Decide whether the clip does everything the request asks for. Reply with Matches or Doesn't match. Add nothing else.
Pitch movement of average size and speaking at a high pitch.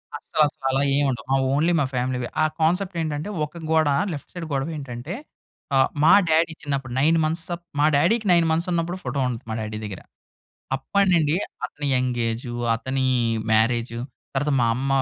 Doesn't match